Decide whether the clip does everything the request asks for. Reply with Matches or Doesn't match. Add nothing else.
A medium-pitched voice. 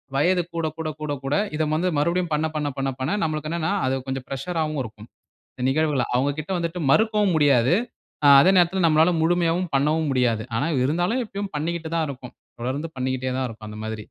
Matches